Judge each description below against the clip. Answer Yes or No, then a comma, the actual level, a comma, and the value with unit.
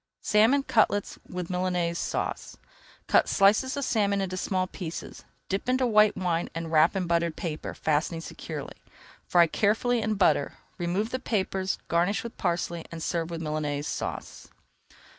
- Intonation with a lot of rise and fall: No, average, 3.9 semitones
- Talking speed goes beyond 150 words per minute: Yes, average, 160 wpm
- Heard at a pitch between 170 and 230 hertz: Yes, medium, 185 Hz